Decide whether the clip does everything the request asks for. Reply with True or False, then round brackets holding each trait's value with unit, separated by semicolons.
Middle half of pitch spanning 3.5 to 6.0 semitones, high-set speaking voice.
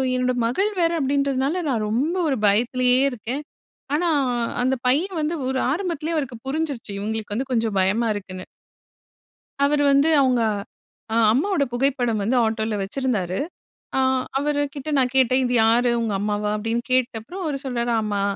True (4.1 semitones; 255 Hz)